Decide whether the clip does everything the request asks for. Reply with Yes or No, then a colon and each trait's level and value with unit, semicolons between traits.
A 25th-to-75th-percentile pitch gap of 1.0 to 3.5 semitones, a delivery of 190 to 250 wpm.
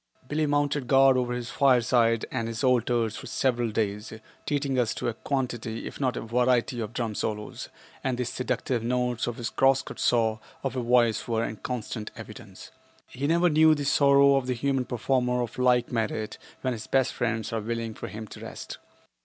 Yes: narrow, 2.6 semitones; average, 195 wpm